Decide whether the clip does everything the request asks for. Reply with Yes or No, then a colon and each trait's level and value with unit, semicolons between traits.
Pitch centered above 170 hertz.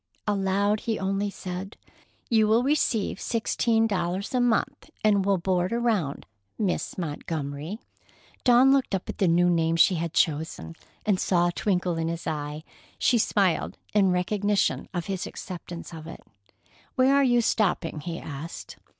Yes: high, 190 Hz